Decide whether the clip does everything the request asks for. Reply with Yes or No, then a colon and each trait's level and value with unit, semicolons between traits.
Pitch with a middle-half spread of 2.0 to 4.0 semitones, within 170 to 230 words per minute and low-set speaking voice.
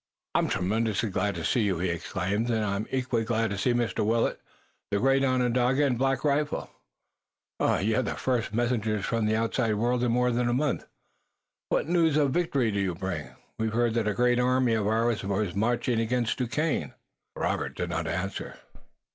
Yes: average, 3.4 semitones; average, 180 wpm; low, 115 Hz